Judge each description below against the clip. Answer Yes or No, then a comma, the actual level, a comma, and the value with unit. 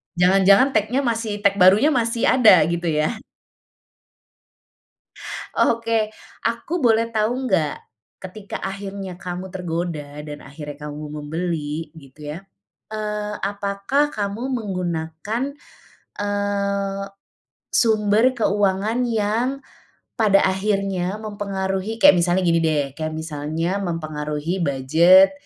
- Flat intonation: No, average, 4.2 semitones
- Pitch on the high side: Yes, high, 195 Hz